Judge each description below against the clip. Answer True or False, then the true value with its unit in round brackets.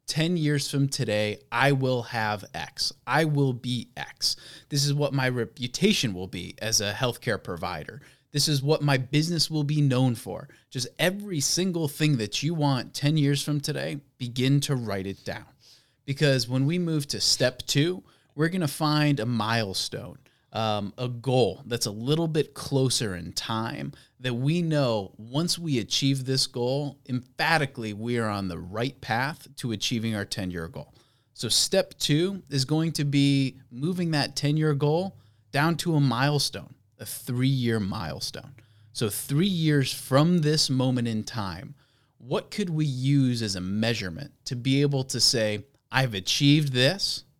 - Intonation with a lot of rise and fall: False (4.0 semitones)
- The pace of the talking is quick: False (165 wpm)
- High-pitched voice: False (135 Hz)